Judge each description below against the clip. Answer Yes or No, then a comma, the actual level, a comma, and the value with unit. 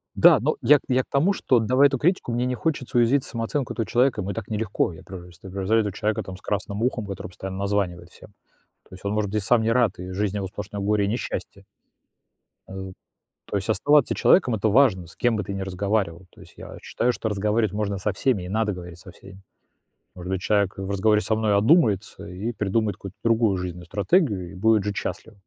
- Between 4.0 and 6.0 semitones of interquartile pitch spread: No, average, 3.2 semitones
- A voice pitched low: Yes, low, 105 Hz